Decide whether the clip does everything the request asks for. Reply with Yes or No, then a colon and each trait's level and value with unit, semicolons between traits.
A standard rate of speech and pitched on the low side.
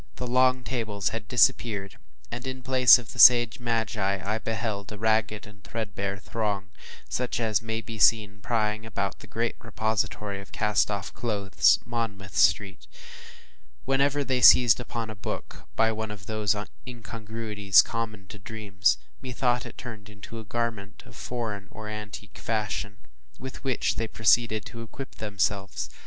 Yes: average, 150 wpm; low, 110 Hz